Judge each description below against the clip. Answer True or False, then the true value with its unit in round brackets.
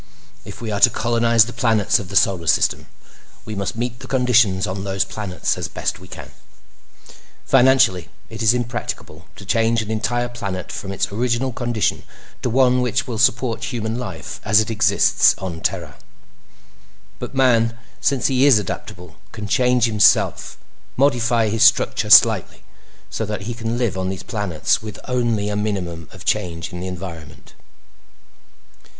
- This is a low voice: True (110 Hz)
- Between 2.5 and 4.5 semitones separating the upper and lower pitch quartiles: True (3.9 semitones)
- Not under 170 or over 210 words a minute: False (155 wpm)